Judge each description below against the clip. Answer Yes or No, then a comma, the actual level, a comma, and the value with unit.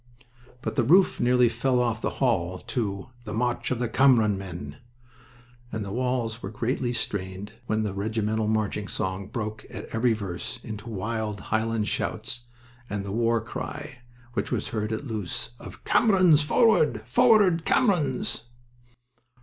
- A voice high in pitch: No, low, 110 Hz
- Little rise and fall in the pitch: No, average, 3.0 semitones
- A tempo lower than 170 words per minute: Yes, average, 150 wpm